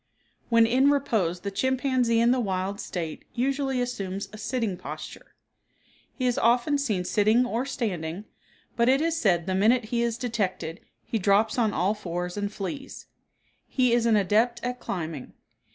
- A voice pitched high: Yes, high, 225 Hz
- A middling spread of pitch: Yes, average, 4.3 semitones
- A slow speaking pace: No, average, 165 wpm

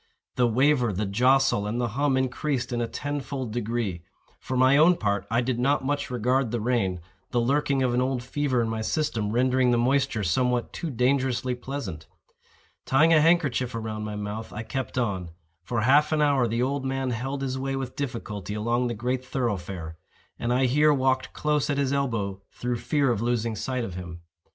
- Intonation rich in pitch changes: No, average, 3.3 semitones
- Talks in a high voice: No, low, 125 Hz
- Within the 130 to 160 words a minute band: No, average, 190 wpm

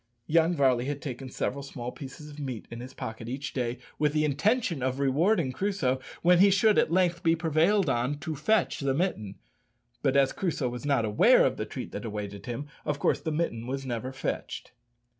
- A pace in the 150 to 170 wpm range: No, average, 200 wpm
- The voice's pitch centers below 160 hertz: Yes, medium, 140 Hz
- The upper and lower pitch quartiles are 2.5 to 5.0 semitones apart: Yes, average, 4.6 semitones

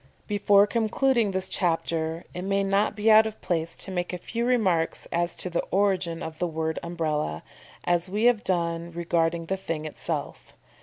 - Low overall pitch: No, medium, 180 Hz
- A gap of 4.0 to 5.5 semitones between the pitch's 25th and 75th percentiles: No, average, 3.6 semitones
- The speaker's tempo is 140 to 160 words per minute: No, average, 175 wpm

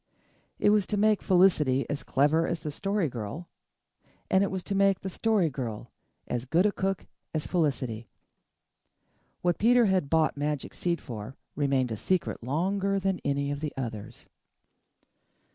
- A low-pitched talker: No, medium, 160 Hz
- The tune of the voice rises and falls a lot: Yes, wide, 6.0 semitones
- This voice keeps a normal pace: Yes, average, 160 wpm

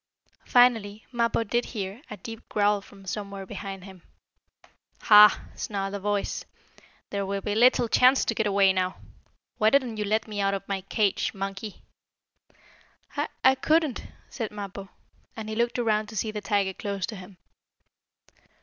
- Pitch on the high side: Yes, high, 210 Hz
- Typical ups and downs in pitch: No, narrow, 2.3 semitones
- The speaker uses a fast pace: No, average, 160 wpm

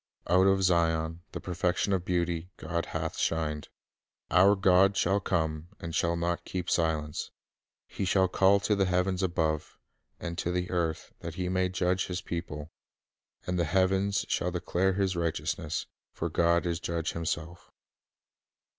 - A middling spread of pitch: No, narrow, 1.9 semitones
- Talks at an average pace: Yes, average, 155 wpm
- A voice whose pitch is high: No, very low, 90 Hz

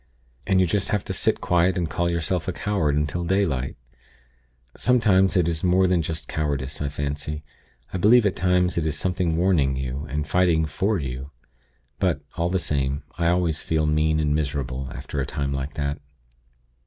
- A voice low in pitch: Yes, very low, 80 Hz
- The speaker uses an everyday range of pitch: Yes, average, 4.0 semitones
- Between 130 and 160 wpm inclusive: No, average, 180 wpm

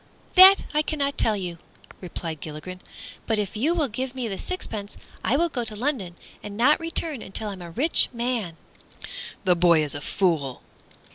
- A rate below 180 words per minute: No, average, 185 wpm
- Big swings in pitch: Yes, wide, 7.8 semitones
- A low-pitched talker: No, high, 215 Hz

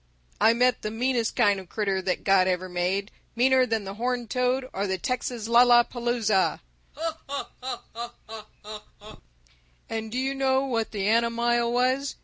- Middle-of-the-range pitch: No, high, 235 Hz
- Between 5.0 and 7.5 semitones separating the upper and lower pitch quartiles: No, average, 3.3 semitones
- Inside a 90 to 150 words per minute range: Yes, average, 140 wpm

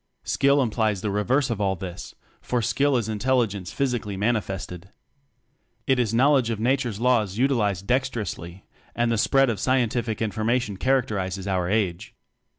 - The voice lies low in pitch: Yes, low, 110 Hz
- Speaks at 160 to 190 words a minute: No, average, 150 wpm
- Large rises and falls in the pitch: No, average, 4.3 semitones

